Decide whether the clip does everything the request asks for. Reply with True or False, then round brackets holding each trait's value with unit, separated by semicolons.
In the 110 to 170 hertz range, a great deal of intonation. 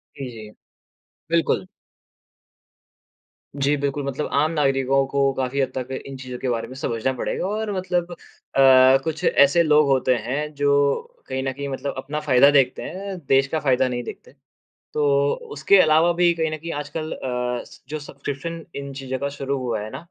False (140 Hz; 2.8 semitones)